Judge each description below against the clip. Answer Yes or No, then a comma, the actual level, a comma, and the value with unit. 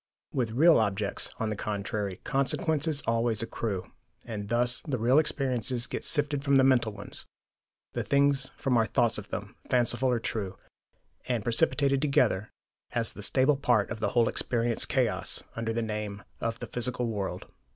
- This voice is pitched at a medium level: No, low, 120 Hz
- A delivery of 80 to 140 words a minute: No, average, 165 wpm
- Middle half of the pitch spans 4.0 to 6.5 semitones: No, average, 3.6 semitones